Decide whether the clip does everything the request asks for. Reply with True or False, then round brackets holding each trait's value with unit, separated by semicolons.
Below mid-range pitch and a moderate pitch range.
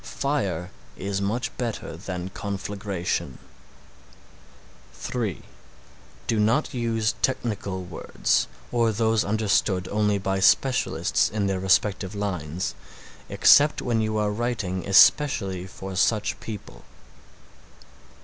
True (105 Hz; 3.1 semitones)